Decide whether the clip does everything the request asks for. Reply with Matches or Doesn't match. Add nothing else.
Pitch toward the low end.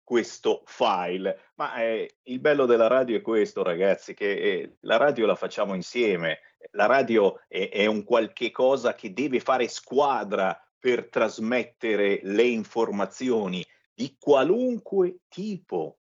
Doesn't match